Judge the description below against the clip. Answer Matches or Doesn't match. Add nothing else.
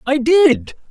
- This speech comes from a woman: Doesn't match